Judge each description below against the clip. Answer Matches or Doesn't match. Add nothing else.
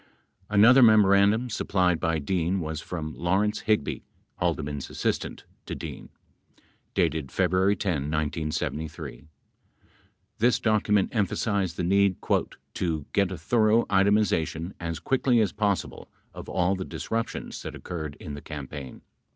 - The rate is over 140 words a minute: Doesn't match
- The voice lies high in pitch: Doesn't match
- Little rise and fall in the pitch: Doesn't match